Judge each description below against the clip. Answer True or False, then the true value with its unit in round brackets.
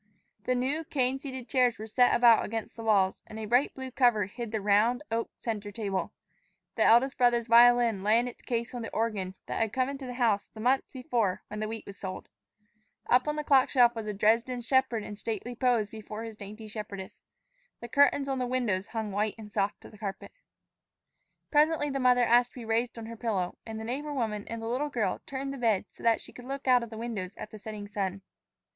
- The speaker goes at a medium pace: False (225 wpm)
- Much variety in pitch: False (2.9 semitones)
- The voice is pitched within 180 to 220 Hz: False (230 Hz)